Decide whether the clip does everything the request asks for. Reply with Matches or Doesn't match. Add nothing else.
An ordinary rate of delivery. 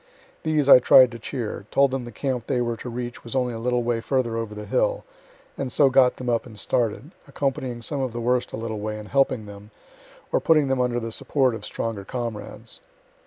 Doesn't match